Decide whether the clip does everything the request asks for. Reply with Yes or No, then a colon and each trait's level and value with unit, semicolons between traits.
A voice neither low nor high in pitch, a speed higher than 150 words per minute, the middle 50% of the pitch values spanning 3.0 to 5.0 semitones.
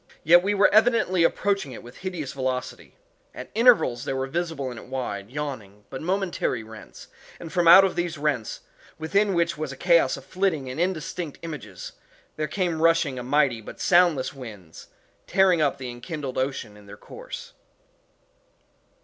No: medium, 150 Hz; average, 165 wpm; wide, 5.5 semitones